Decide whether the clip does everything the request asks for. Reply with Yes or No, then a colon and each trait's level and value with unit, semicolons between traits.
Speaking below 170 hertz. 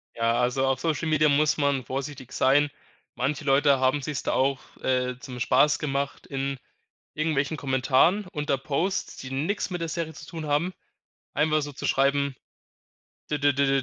Yes: medium, 140 Hz